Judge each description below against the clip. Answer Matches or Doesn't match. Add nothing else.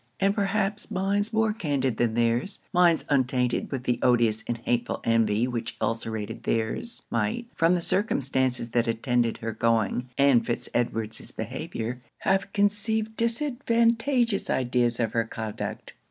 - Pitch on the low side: Matches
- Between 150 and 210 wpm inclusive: Doesn't match